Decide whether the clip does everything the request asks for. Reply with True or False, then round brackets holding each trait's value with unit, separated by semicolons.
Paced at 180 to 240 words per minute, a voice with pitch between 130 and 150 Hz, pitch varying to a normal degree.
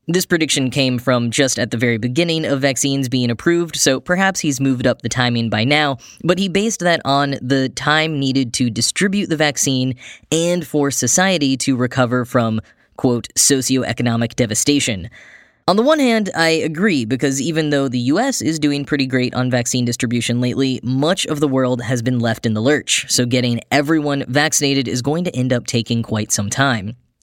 True (185 wpm; 135 Hz; 3.5 semitones)